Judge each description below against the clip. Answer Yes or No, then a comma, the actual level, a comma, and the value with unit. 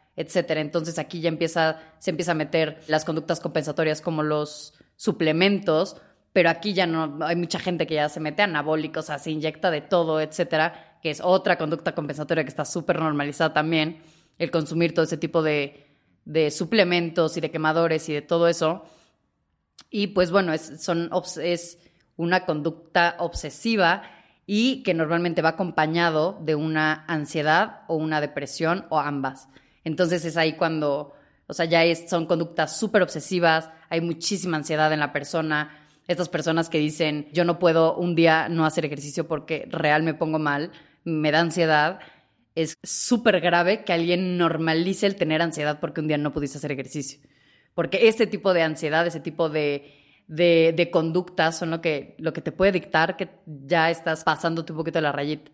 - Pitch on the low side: No, medium, 160 Hz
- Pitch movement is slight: Yes, narrow, 1.9 semitones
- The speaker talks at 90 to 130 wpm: No, average, 175 wpm